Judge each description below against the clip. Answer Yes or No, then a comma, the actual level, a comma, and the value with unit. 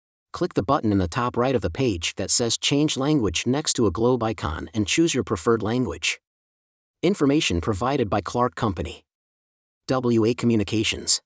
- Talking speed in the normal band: Yes, average, 165 wpm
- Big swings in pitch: Yes, wide, 5.9 semitones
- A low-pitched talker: Yes, low, 115 Hz